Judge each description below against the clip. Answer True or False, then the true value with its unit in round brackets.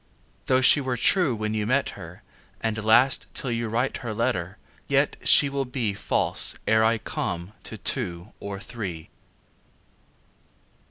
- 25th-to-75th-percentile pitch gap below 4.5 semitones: True (3.9 semitones)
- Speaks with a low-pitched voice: True (110 Hz)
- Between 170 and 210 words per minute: False (150 wpm)